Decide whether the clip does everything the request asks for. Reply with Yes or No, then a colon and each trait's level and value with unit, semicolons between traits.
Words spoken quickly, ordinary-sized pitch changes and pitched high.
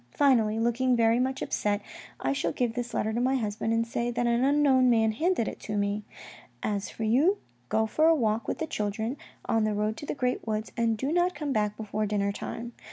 Yes: fast, 225 wpm; average, 3.2 semitones; high, 230 Hz